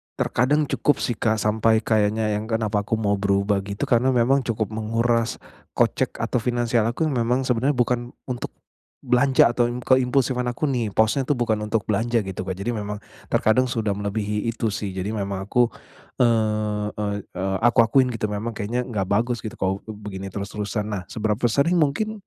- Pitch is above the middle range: No, low, 110 Hz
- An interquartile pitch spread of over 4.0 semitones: No, average, 2.7 semitones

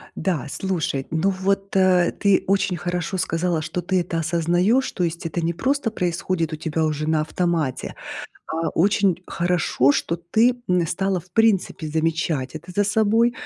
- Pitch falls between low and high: Yes, medium, 175 Hz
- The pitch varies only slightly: No, average, 3.1 semitones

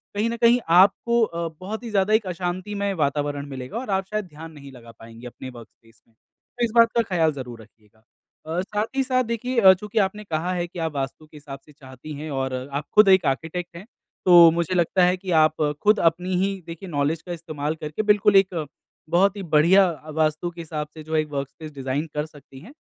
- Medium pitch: Yes, medium, 170 Hz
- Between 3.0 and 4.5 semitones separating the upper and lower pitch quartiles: No, average, 4.9 semitones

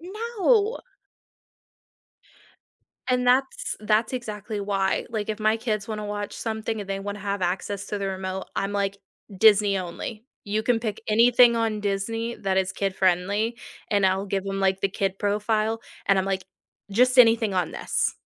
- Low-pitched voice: No, high, 210 Hz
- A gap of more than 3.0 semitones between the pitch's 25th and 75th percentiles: No, narrow, 2.6 semitones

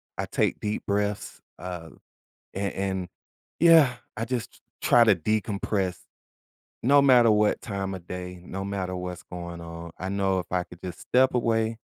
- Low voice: Yes, low, 100 Hz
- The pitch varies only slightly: No, average, 3.7 semitones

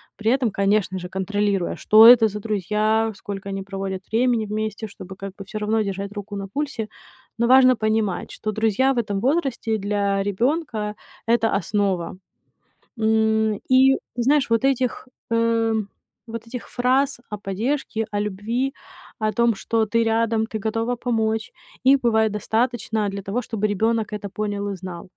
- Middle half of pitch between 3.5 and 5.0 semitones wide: No, narrow, 2.4 semitones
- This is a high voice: Yes, high, 220 Hz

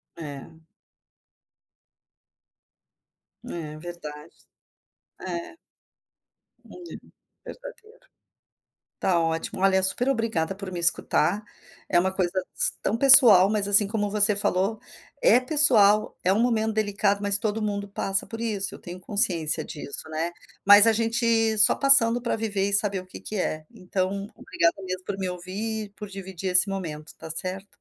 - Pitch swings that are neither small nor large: Yes, average, 3.4 semitones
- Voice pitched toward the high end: Yes, high, 200 Hz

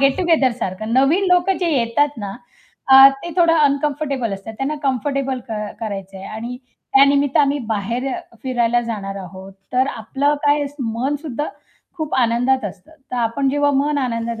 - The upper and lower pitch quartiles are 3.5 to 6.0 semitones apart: Yes, average, 4.0 semitones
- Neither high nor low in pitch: No, very high, 260 Hz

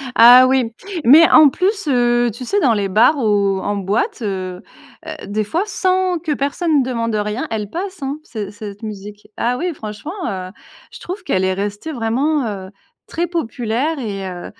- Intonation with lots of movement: Yes, wide, 6.9 semitones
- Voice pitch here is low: No, high, 235 Hz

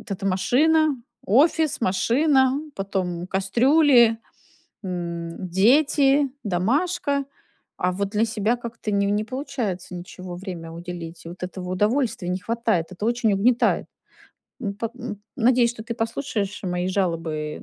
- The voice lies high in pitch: Yes, high, 210 Hz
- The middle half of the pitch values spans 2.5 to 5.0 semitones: No, wide, 5.5 semitones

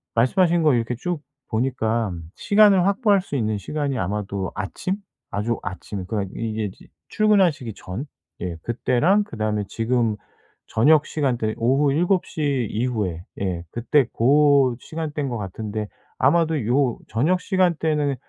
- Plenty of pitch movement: Yes, wide, 6.4 semitones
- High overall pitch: No, low, 125 Hz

